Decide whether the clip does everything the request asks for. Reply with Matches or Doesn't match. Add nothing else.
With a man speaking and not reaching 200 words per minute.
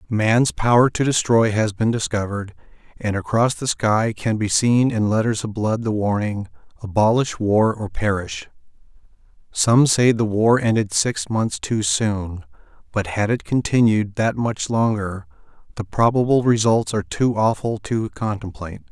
Matches